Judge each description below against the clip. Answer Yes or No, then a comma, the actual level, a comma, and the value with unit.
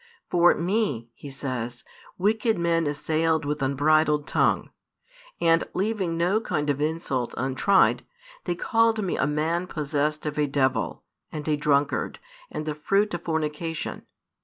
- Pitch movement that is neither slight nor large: Yes, average, 3.1 semitones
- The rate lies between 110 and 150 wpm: Yes, average, 140 wpm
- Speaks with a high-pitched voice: No, medium, 155 Hz